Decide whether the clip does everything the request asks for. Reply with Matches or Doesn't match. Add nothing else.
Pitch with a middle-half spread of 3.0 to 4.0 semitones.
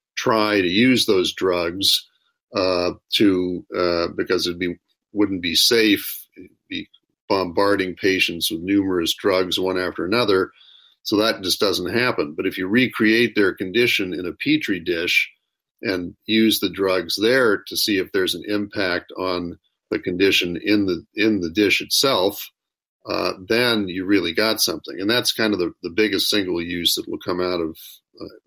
Doesn't match